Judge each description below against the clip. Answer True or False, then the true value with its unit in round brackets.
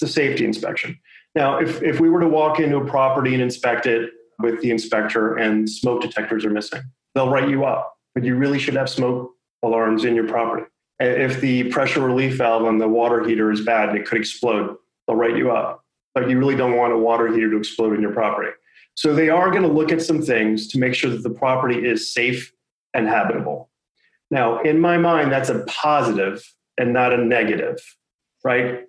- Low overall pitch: True (125 Hz)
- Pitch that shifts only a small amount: False (3.1 semitones)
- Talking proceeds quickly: True (210 wpm)